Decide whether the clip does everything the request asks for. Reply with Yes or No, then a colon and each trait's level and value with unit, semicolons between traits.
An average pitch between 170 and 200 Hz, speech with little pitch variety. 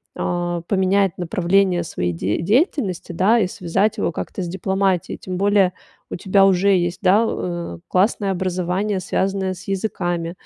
Yes: medium, 185 Hz; narrow, 2.1 semitones